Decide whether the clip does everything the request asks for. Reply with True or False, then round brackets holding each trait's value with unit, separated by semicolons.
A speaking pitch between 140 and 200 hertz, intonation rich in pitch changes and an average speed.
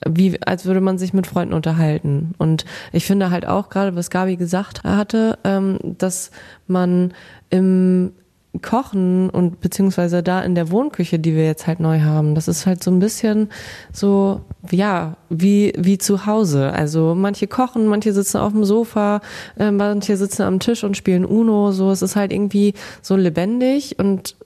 False (190 Hz; 2.5 semitones; 170 wpm)